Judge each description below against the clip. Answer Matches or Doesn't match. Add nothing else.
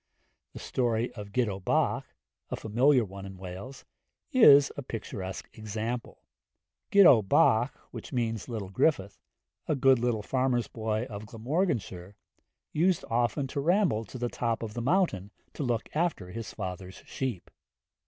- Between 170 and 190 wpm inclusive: Doesn't match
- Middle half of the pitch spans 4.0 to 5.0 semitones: Matches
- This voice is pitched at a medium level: Doesn't match